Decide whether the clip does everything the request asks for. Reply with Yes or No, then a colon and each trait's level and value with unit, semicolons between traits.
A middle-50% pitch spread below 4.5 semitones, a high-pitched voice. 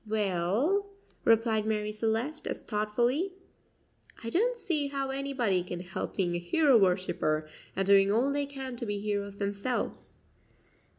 No: wide, 5.5 semitones; high, 220 Hz